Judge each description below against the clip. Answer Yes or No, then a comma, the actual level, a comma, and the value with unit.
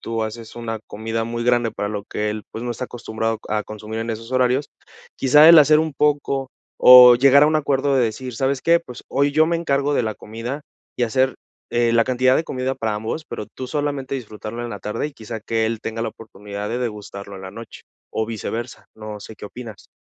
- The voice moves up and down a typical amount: Yes, average, 3.4 semitones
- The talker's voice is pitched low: Yes, low, 120 Hz